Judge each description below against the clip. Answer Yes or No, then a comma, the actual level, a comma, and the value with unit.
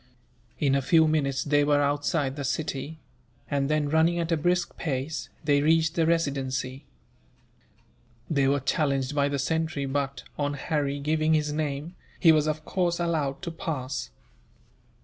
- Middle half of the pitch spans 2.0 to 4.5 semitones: Yes, narrow, 2.5 semitones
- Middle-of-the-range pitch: Yes, medium, 145 Hz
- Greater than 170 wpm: No, average, 155 wpm